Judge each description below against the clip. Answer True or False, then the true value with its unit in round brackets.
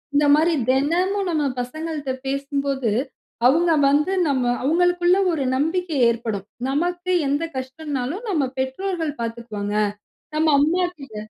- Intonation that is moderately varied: True (4.7 semitones)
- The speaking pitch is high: True (290 Hz)